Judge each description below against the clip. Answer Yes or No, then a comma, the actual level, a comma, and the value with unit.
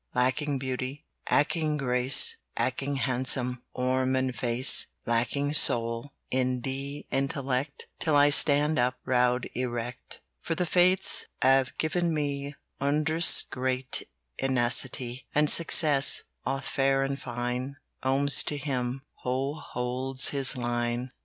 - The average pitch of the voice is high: No, low, 130 Hz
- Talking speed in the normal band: No, slow, 115 wpm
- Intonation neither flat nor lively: No, narrow, 2.2 semitones